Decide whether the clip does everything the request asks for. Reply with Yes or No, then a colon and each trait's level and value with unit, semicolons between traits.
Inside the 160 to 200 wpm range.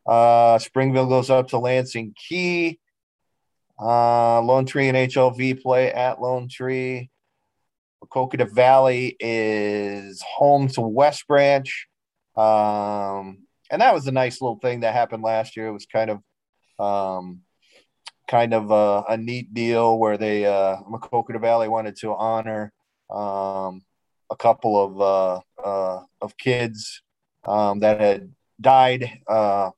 No: slow, 135 wpm